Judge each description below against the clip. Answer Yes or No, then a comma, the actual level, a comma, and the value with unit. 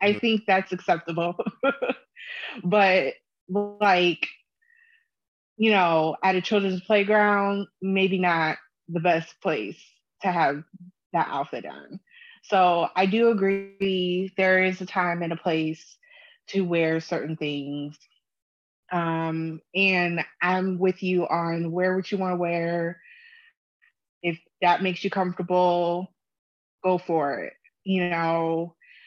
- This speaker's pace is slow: Yes, slow, 120 wpm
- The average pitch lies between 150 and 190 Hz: Yes, medium, 185 Hz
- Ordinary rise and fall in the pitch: Yes, average, 3.0 semitones